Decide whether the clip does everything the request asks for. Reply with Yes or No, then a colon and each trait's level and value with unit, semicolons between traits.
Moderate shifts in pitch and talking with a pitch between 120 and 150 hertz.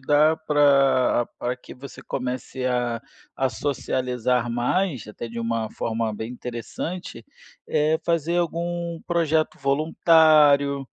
Yes: average, 4.6 semitones; low, 135 Hz